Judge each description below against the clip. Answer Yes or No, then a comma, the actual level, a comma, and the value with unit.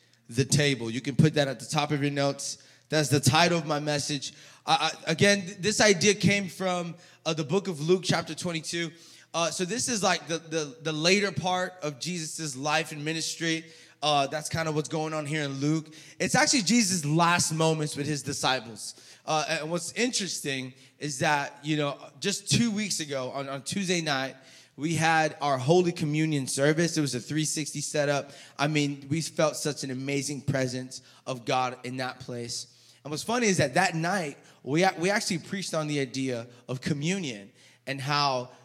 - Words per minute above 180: Yes, average, 190 wpm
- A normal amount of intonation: Yes, average, 3.5 semitones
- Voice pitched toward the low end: No, medium, 155 Hz